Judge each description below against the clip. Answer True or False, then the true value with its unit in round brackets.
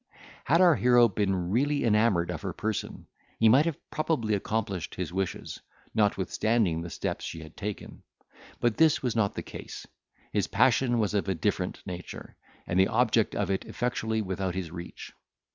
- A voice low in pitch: True (105 Hz)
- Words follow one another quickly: False (170 wpm)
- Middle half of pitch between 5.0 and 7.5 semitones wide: False (4.1 semitones)